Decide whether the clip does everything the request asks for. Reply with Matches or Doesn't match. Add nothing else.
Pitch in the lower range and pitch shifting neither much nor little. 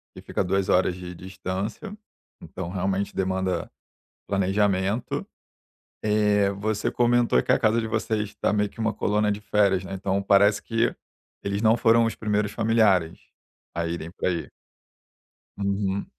Doesn't match